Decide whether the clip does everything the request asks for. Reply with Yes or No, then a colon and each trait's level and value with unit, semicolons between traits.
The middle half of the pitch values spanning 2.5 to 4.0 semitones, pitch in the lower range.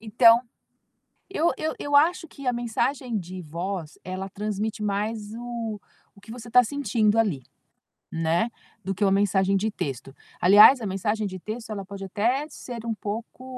No: average, 3.7 semitones; high, 215 Hz